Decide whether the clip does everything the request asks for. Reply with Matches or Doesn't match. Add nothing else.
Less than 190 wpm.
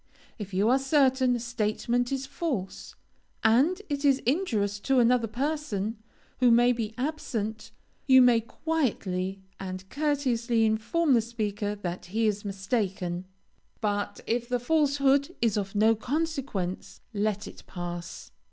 Matches